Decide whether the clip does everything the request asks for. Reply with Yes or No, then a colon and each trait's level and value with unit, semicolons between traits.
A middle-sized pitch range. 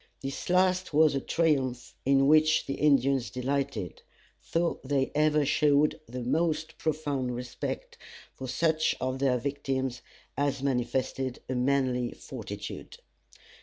Yes: average, 3.1 semitones